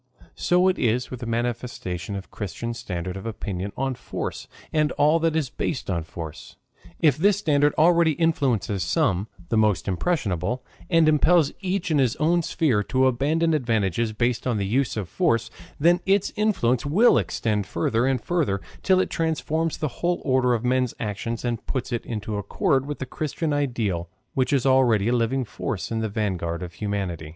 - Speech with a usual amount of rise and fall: No, wide, 6.6 semitones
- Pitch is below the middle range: Yes, low, 125 Hz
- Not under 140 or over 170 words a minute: No, average, 180 wpm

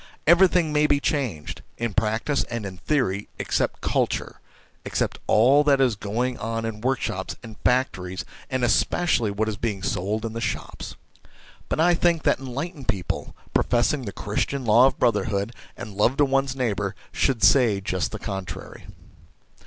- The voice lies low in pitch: Yes, low, 115 Hz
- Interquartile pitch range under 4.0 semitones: No, average, 4.8 semitones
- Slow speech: No, average, 165 wpm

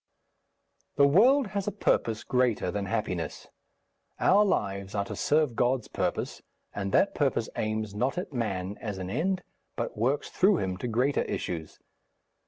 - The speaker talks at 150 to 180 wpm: Yes, average, 155 wpm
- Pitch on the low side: Yes, low, 115 Hz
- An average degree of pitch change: No, wide, 7.1 semitones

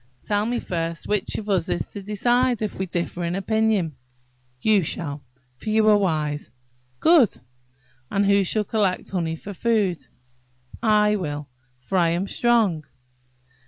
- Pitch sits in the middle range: No, high, 195 Hz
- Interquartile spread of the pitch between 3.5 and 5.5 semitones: Yes, average, 4.1 semitones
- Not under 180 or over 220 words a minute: No, average, 150 wpm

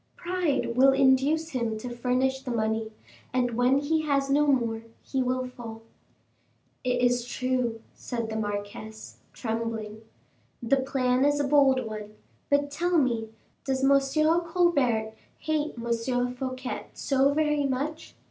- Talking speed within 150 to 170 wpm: No, average, 140 wpm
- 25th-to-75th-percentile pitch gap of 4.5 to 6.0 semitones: No, average, 3.3 semitones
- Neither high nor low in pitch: No, very high, 255 Hz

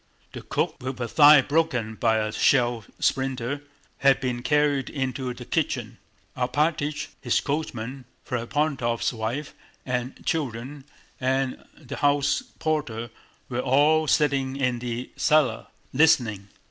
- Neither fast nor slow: No, slow, 120 wpm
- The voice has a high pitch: No, low, 130 Hz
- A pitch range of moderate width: Yes, average, 3.3 semitones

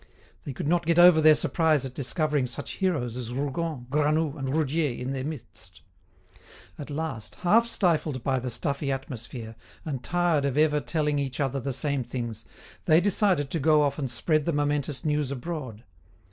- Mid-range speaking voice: Yes, medium, 145 Hz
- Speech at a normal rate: Yes, average, 175 wpm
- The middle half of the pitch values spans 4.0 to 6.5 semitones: No, average, 3.3 semitones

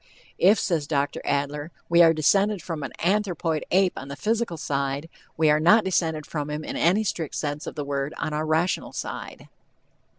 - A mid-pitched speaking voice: Yes, medium, 160 Hz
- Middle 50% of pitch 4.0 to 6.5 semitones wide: No, average, 3.6 semitones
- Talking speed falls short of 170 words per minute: No, average, 190 wpm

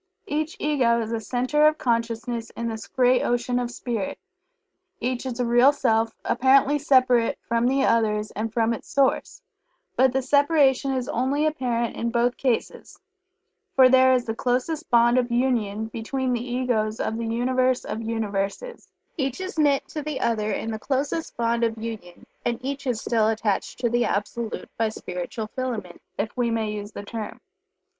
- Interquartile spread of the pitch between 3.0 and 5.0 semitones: No, narrow, 2.6 semitones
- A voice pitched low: No, high, 240 Hz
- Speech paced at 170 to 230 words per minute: Yes, average, 175 wpm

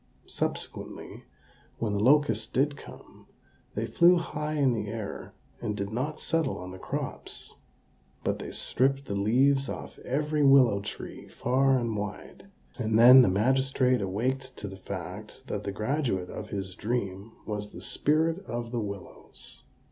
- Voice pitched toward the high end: No, low, 120 Hz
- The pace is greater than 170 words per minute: No, average, 155 wpm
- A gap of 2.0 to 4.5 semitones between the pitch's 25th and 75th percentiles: No, average, 4.9 semitones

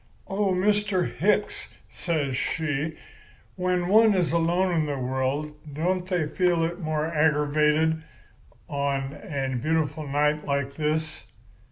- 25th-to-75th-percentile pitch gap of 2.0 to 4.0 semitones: Yes, average, 3.6 semitones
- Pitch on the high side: No, medium, 160 Hz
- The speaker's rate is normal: No, slow, 125 wpm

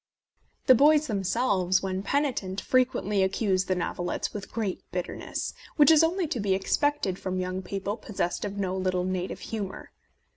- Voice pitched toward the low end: No, high, 195 Hz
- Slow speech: No, average, 160 wpm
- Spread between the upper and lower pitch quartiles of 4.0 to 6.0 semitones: Yes, average, 5.1 semitones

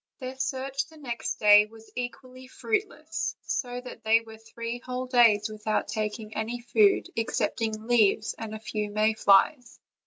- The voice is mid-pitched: No, high, 230 Hz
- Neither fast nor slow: Yes, average, 155 wpm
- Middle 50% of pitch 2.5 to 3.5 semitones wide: Yes, average, 2.8 semitones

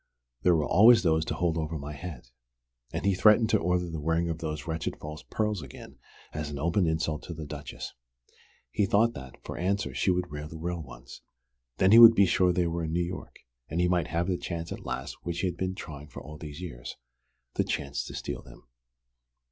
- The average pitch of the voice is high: No, very low, 85 Hz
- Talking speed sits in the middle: No, fast, 220 wpm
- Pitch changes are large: No, average, 2.9 semitones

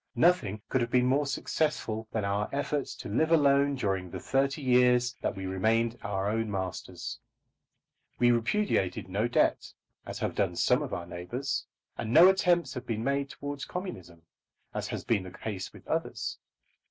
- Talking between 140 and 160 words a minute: No, average, 170 wpm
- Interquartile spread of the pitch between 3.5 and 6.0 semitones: Yes, wide, 5.5 semitones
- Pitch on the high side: No, low, 120 Hz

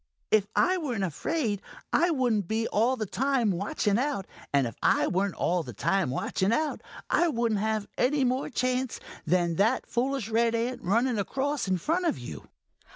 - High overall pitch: Yes, high, 225 Hz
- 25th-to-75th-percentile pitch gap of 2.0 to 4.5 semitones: No, average, 5.1 semitones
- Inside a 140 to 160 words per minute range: No, average, 175 wpm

